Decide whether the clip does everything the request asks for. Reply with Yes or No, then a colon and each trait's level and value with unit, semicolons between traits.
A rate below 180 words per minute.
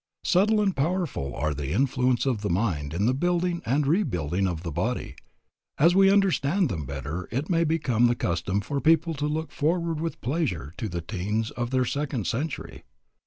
No: average, 185 wpm